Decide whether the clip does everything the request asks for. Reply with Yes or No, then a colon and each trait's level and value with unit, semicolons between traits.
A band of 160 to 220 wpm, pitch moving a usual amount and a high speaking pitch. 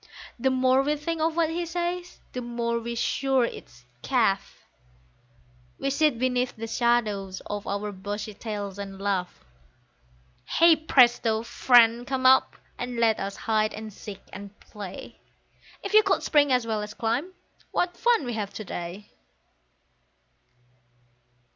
No: average, 145 wpm; average, 4.7 semitones; high, 235 Hz